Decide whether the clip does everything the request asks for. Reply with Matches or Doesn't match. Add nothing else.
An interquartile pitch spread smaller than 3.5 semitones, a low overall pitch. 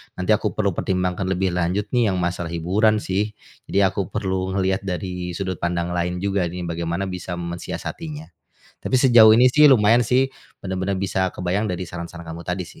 Matches